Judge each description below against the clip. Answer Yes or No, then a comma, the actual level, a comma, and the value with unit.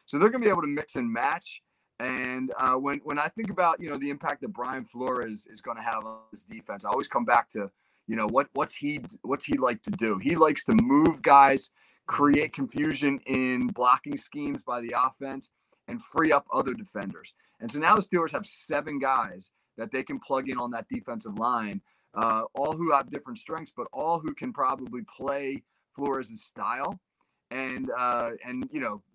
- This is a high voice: No, medium, 140 Hz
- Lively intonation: Yes, wide, 6.5 semitones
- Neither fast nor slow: No, fast, 210 wpm